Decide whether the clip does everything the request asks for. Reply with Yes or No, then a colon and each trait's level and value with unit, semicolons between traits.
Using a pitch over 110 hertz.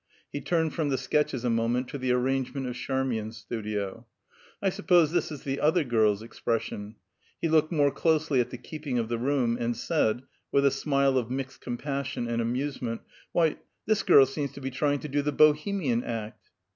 Yes: low, 135 Hz